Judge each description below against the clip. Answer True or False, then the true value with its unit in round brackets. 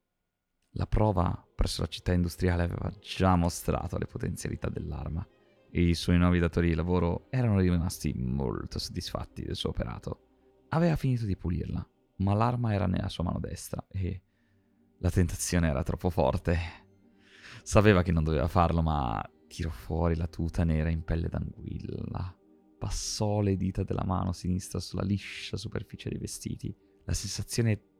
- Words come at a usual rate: True (150 wpm)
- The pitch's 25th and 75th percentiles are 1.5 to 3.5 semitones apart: True (2.9 semitones)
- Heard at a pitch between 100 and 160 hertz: False (90 Hz)